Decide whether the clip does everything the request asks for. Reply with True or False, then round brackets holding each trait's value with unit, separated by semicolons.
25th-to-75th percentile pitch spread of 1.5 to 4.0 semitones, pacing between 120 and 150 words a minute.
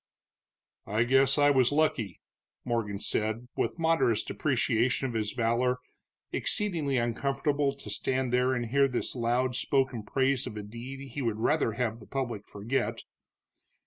True (3.1 semitones; 145 wpm)